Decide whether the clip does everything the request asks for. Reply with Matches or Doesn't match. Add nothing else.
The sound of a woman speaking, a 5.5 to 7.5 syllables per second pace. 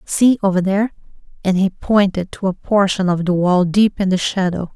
Doesn't match